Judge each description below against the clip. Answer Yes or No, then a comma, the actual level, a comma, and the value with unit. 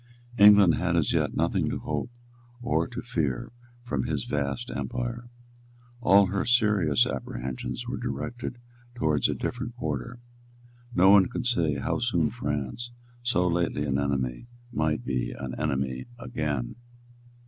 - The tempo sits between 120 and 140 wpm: Yes, slow, 135 wpm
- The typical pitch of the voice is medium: No, very low, 85 Hz